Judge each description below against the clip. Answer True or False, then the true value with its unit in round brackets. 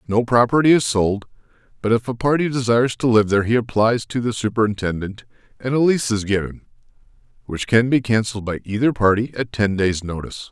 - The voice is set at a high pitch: False (115 Hz)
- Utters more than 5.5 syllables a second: True (6.0 syllables/s)